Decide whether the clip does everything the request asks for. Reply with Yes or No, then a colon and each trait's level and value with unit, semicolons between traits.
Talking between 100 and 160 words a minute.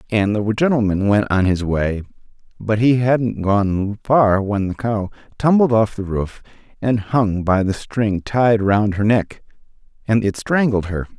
No: average, 170 wpm